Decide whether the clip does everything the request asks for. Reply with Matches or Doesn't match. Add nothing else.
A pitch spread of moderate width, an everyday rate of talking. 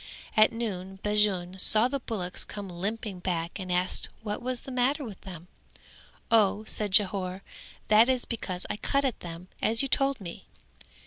Matches